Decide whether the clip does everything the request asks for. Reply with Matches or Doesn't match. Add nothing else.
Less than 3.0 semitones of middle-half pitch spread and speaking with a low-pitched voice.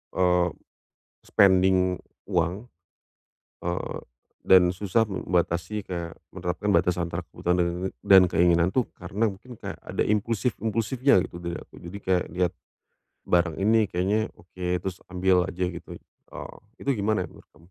Matches